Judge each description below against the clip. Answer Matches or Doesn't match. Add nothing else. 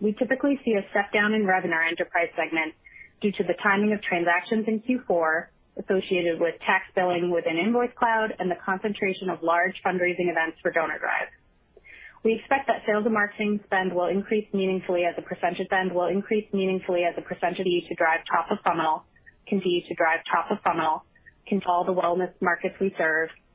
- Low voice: Doesn't match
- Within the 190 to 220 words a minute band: Matches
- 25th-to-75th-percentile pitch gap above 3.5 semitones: Doesn't match